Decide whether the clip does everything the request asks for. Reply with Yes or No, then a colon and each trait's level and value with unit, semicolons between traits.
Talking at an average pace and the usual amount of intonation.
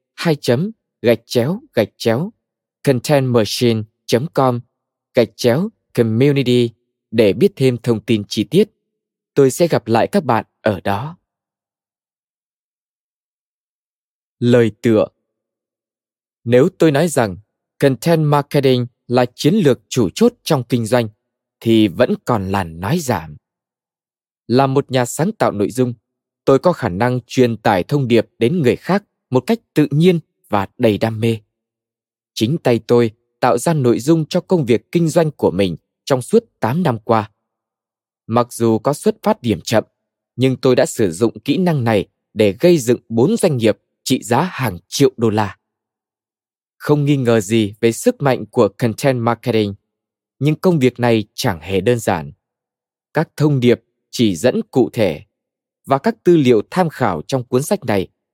No: slow, 160 wpm; average, 4.6 semitones